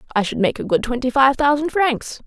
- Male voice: No, female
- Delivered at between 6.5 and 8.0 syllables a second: No, 5.8 syllables/s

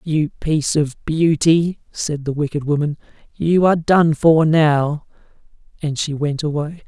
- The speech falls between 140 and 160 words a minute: Yes, average, 150 wpm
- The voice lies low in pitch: No, medium, 155 Hz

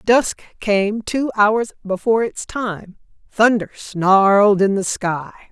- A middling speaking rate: No, slow, 130 wpm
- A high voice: Yes, high, 205 Hz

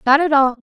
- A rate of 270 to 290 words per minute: Yes, fast, 285 wpm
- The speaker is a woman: Yes, female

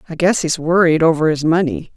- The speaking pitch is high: No, medium, 165 Hz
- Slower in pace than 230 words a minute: No, fast, 245 wpm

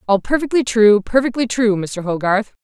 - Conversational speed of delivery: Yes, average, 160 wpm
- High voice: Yes, high, 220 Hz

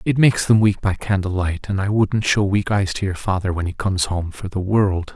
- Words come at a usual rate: No, fast, 270 wpm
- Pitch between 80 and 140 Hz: Yes, low, 100 Hz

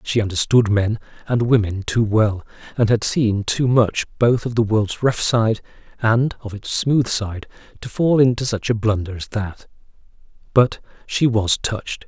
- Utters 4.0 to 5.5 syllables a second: Yes, 4.3 syllables/s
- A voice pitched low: Yes, low, 110 Hz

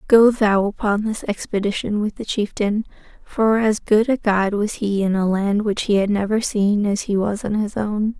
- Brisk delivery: Yes, fast, 210 wpm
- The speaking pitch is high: Yes, high, 210 Hz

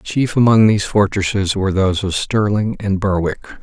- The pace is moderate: Yes, average, 165 wpm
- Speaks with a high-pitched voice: No, low, 100 Hz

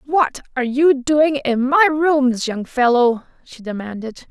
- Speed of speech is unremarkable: Yes, average, 155 wpm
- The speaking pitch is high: Yes, very high, 265 Hz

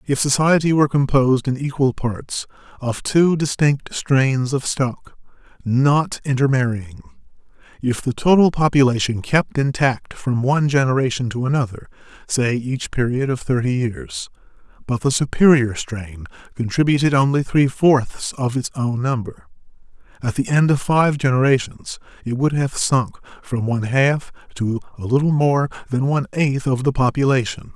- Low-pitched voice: Yes, low, 130 Hz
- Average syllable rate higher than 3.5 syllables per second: Yes, 4.5 syllables/s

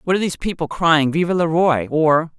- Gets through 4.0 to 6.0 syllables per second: Yes, 5.5 syllables/s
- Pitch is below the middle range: No, medium, 160 Hz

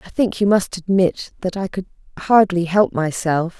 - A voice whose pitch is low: No, medium, 185 Hz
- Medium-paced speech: Yes, average, 185 wpm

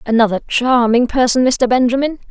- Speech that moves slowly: Yes, slow, 130 wpm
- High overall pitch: Yes, high, 245 Hz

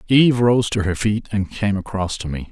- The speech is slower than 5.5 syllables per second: Yes, 5.2 syllables/s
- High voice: No, low, 105 Hz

